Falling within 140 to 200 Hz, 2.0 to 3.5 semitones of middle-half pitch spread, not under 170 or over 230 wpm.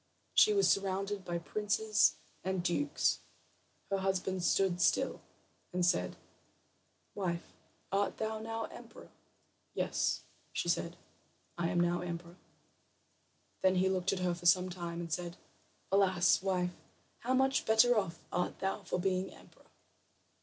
No: medium, 185 Hz; narrow, 2.4 semitones; slow, 135 wpm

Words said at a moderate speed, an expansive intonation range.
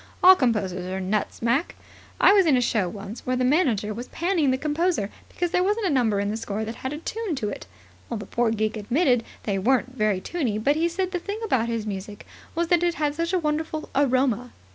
No: fast, 225 wpm; wide, 7.6 semitones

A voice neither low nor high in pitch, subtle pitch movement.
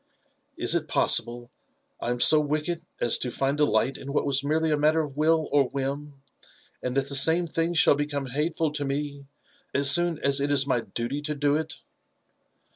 Yes: medium, 145 Hz; narrow, 2.0 semitones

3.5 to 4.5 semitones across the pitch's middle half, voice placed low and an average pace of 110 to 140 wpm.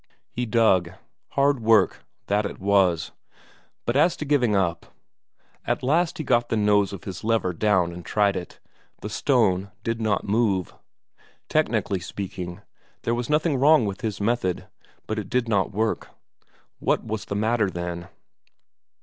No: average, 3.8 semitones; low, 105 Hz; average, 155 wpm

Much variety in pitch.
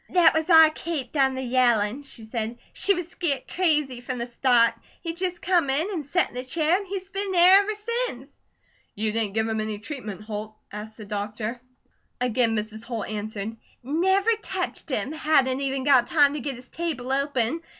Yes: wide, 6.8 semitones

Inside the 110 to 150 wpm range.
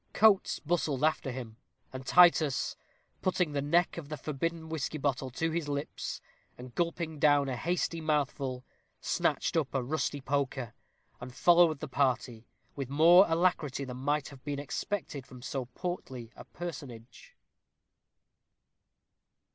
Yes: average, 140 wpm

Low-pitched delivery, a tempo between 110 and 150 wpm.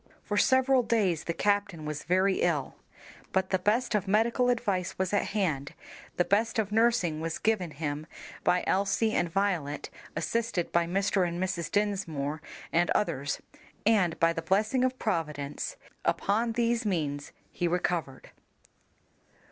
No: high, 190 Hz; average, 145 wpm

